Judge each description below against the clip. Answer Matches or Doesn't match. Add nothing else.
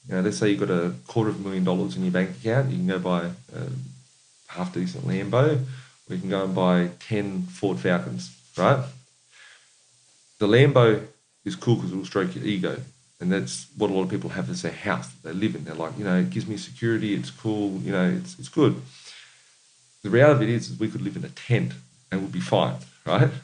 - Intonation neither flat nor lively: Doesn't match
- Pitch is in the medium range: Doesn't match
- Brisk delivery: Matches